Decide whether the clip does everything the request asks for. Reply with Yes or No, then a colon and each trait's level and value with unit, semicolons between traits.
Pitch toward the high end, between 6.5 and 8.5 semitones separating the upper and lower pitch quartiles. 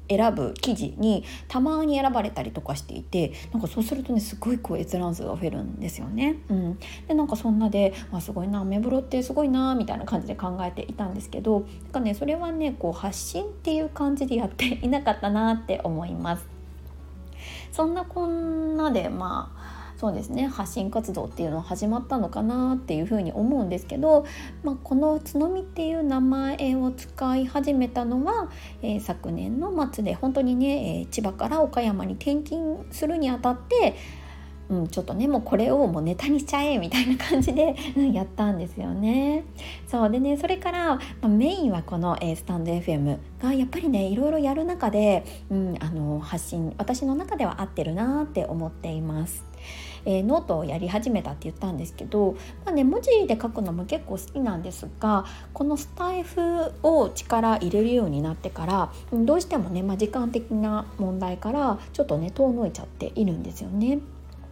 Yes: high, 235 Hz; wide, 7.0 semitones